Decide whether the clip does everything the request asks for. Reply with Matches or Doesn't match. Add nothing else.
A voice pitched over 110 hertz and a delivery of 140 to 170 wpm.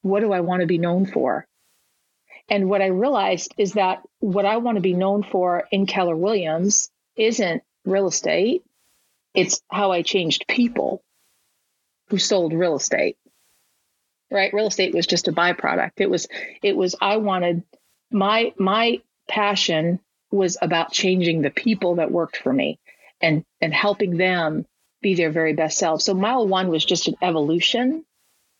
Matches